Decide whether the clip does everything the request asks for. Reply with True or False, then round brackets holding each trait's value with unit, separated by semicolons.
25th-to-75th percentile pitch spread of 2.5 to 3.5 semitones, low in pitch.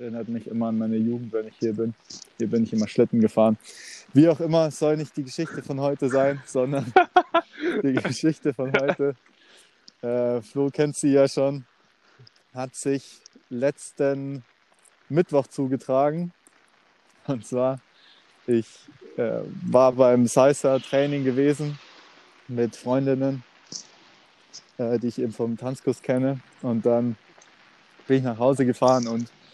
True (2.9 semitones; 130 Hz)